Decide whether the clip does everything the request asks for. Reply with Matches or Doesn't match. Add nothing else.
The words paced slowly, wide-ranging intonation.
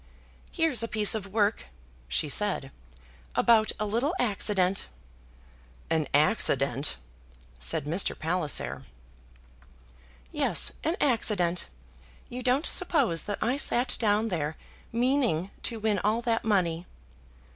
Matches